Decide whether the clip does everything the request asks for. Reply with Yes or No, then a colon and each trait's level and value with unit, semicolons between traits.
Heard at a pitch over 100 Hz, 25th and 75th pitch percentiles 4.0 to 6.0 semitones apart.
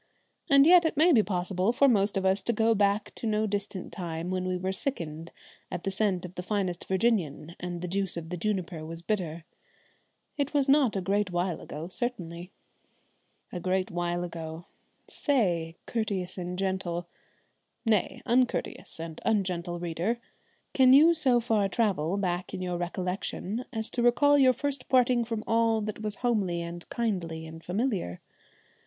Yes: high, 190 Hz; average, 4.6 semitones